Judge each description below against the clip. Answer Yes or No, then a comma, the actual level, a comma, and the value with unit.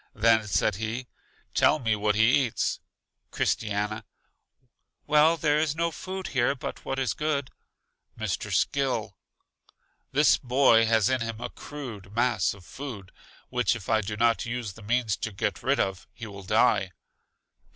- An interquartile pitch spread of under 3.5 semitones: No, average, 4.1 semitones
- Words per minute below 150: No, average, 155 wpm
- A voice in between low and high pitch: No, low, 115 Hz